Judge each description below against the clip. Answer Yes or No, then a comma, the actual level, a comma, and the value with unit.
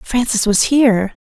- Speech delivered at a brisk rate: No, average, 145 wpm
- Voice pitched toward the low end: No, high, 230 Hz